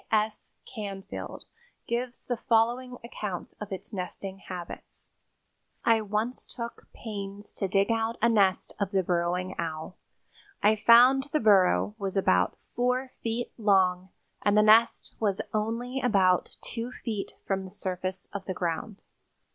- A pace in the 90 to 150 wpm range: Yes, average, 145 wpm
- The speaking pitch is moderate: No, high, 205 Hz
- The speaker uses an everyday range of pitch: Yes, average, 3.5 semitones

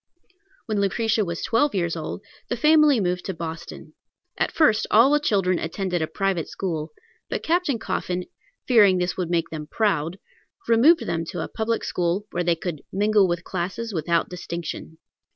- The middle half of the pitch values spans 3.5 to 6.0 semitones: Yes, average, 4.7 semitones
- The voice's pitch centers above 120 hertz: Yes, medium, 185 Hz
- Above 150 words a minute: Yes, average, 170 wpm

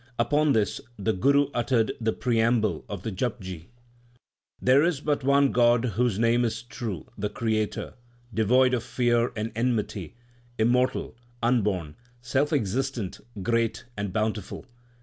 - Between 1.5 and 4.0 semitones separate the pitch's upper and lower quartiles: Yes, average, 3.0 semitones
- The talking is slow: Yes, slow, 130 wpm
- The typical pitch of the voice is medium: No, low, 115 Hz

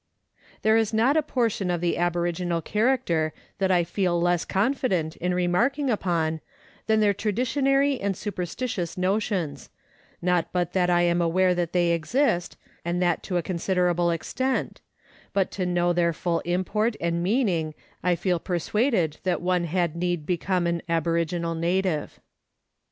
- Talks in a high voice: No, medium, 180 Hz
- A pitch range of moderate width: Yes, average, 3.0 semitones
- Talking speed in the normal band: Yes, average, 150 wpm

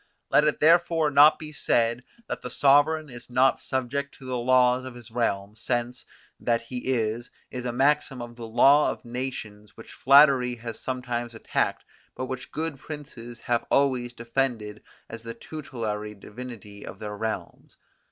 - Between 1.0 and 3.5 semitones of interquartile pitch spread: Yes, average, 2.8 semitones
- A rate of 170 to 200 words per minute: No, average, 160 wpm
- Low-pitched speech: Yes, low, 125 Hz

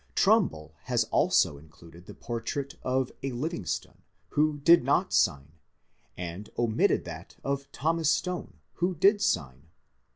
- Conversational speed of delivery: No, slow, 130 wpm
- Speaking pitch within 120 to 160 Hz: Yes, low, 135 Hz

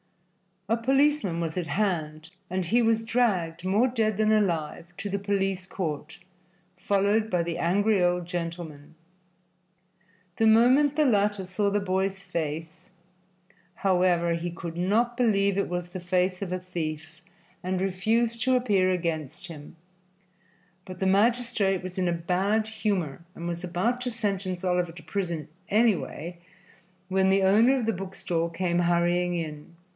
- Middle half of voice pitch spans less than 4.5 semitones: Yes, average, 3.5 semitones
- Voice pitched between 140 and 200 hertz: Yes, medium, 185 Hz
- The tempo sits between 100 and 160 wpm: Yes, average, 150 wpm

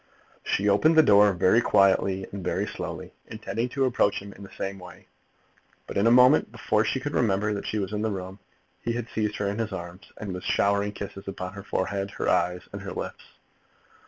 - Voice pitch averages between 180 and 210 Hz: No, low, 100 Hz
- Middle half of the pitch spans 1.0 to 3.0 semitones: Yes, narrow, 2.4 semitones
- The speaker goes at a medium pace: No, fast, 215 wpm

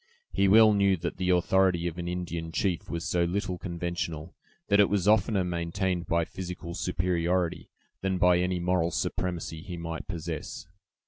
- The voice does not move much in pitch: Yes, narrow, 1.8 semitones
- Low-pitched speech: Yes, very low, 90 Hz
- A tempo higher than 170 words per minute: No, average, 165 wpm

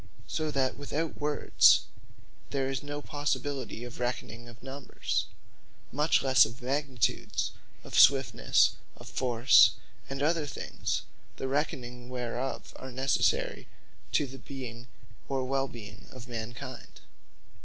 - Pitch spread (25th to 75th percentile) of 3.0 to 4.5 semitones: No, narrow, 2.5 semitones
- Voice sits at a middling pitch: No, low, 130 Hz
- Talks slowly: Yes, slow, 125 wpm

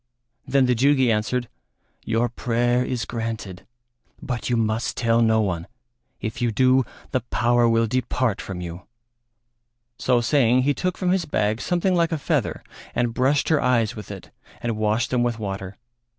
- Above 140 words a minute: Yes, average, 165 wpm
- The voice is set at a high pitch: No, low, 120 Hz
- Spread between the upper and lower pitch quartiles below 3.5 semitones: Yes, average, 2.7 semitones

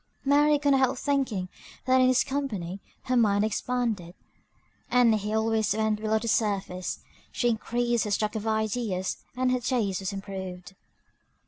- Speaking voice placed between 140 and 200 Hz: No, high, 220 Hz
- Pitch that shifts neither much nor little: Yes, average, 3.9 semitones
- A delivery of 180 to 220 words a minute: No, average, 155 wpm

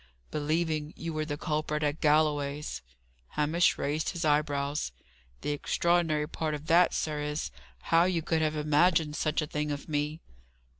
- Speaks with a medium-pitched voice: Yes, medium, 150 Hz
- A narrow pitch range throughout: Yes, narrow, 1.5 semitones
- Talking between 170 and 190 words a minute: No, average, 155 wpm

